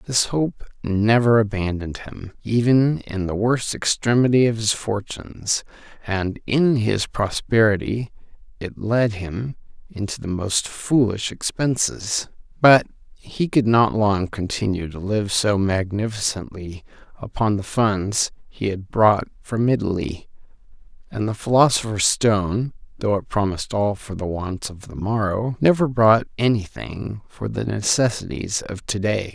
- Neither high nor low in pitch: No, low, 105 Hz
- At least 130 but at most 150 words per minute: Yes, slow, 135 wpm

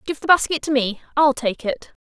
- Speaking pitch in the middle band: No, very high, 280 Hz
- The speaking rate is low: No, fast, 205 wpm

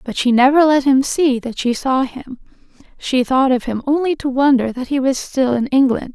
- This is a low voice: No, very high, 265 Hz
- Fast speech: Yes, fast, 225 wpm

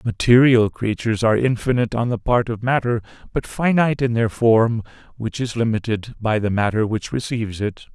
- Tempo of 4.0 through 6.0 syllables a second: Yes, 5.5 syllables/s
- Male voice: Yes, male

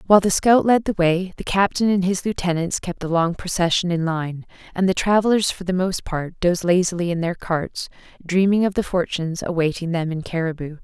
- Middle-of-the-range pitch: Yes, medium, 180 Hz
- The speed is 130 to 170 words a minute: No, fast, 205 wpm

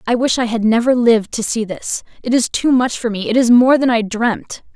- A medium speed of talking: No, fast, 255 wpm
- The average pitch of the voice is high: Yes, high, 235 Hz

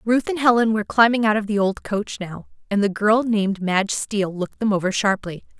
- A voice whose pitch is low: No, high, 210 Hz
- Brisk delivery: Yes, fast, 225 wpm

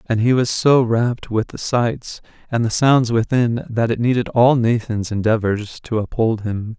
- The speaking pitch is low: Yes, low, 115 Hz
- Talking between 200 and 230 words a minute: No, average, 185 wpm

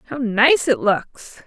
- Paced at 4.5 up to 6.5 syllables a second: No, 2.8 syllables/s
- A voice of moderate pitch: No, high, 245 Hz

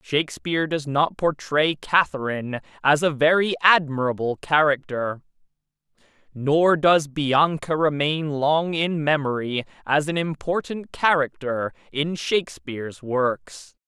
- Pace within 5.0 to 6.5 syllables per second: No, 4.1 syllables/s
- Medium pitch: Yes, medium, 150 Hz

